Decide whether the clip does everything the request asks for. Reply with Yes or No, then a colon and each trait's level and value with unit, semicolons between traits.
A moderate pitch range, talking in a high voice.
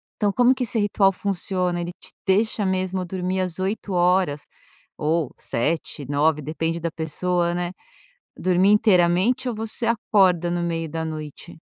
No: average, 3.0 semitones; medium, 180 Hz